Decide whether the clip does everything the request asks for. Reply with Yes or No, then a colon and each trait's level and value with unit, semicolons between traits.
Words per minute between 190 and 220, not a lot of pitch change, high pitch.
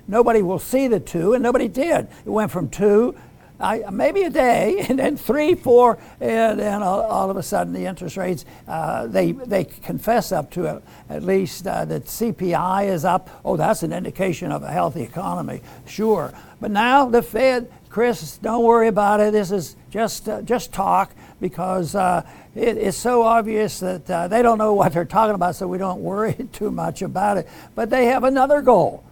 No: average, 195 wpm; average, 4.1 semitones; high, 210 Hz